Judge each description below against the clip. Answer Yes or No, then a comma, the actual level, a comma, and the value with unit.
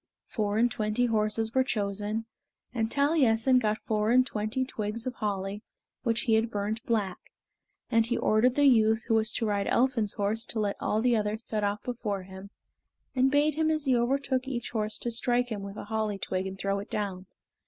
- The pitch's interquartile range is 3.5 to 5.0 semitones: No, average, 2.9 semitones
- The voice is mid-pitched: No, high, 220 Hz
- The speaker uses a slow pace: No, average, 200 wpm